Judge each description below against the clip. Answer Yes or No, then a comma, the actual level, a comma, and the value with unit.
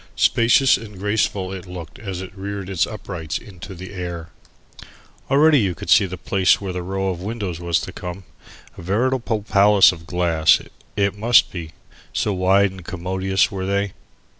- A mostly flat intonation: Yes, narrow, 2.2 semitones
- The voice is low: Yes, very low, 95 Hz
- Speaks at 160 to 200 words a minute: Yes, average, 170 wpm